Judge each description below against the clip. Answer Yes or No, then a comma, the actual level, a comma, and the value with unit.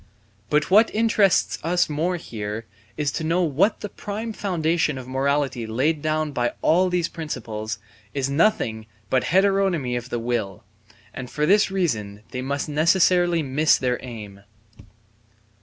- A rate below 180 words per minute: Yes, average, 145 wpm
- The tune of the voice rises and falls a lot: Yes, wide, 6.4 semitones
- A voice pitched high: No, medium, 150 Hz